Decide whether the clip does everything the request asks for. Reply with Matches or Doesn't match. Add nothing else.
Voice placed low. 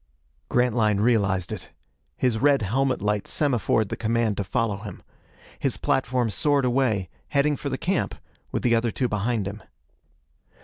Matches